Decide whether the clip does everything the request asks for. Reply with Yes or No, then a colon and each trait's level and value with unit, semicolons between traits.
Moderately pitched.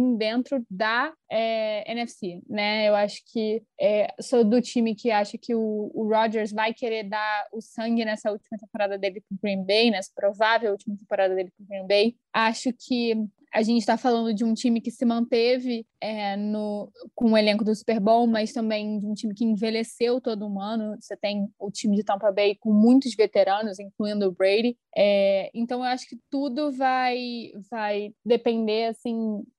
No: high, 220 Hz